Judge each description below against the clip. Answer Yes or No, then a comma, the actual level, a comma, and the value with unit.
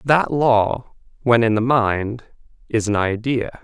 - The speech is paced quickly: No, average, 150 wpm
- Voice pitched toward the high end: No, low, 115 Hz